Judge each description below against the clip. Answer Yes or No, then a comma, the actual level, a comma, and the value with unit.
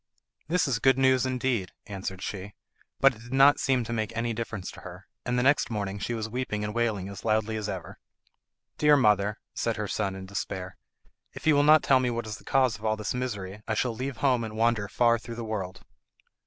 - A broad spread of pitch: No, average, 3.6 semitones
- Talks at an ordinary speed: No, fast, 225 wpm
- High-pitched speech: No, low, 115 Hz